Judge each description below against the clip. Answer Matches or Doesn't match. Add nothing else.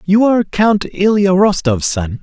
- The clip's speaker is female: Doesn't match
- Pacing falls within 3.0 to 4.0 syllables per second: Doesn't match